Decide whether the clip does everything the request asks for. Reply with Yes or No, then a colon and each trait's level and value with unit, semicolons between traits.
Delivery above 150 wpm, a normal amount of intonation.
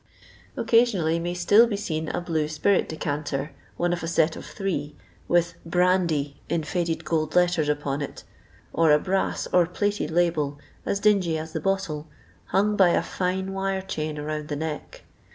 Yes: average, 165 wpm; average, 3.6 semitones